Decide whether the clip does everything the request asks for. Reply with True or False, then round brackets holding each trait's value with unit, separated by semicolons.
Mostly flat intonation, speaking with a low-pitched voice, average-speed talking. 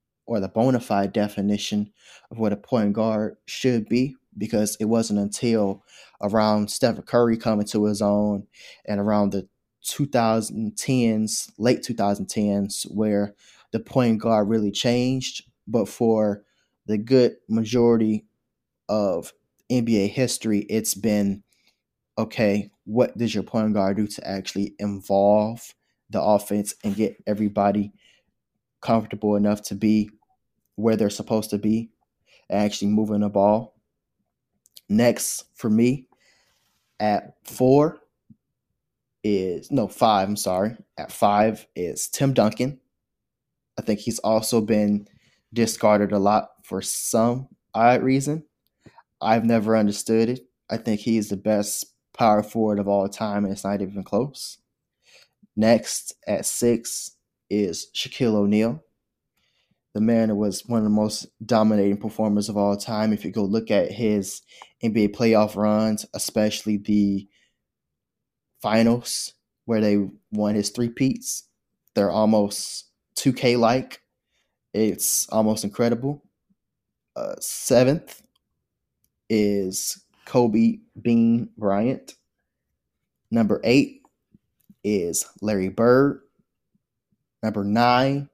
False (2.0 semitones; 110 Hz; 120 wpm)